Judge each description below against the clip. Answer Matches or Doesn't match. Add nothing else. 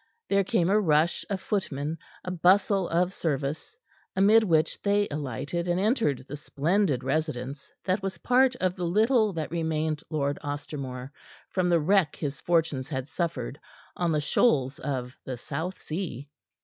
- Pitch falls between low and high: Matches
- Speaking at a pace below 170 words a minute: Matches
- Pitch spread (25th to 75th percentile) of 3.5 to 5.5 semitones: Matches